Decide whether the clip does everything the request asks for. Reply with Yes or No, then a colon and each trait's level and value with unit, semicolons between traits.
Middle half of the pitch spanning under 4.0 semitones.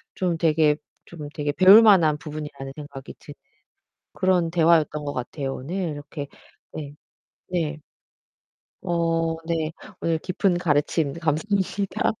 Yes: average, 2.7 semitones